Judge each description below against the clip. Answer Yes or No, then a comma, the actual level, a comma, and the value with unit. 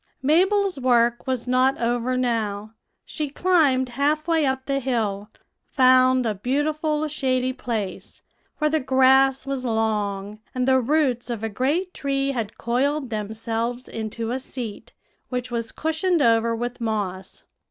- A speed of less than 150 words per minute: Yes, average, 140 wpm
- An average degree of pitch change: Yes, average, 3.3 semitones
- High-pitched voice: Yes, very high, 255 Hz